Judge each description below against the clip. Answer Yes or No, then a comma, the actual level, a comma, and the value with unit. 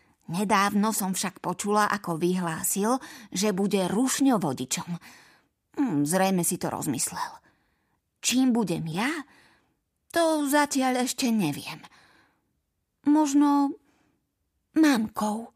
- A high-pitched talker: Yes, high, 210 Hz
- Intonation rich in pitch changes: Yes, wide, 7.2 semitones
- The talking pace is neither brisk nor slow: No, slow, 90 wpm